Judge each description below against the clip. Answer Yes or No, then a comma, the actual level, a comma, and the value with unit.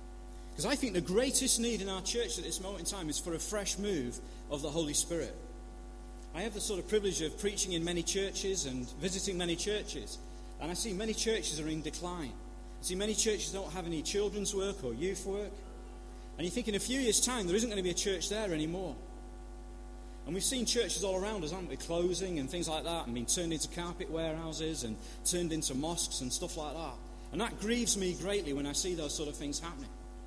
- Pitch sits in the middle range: Yes, medium, 175 Hz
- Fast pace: Yes, fast, 230 wpm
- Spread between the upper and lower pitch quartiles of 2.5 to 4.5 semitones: No, average, 5.2 semitones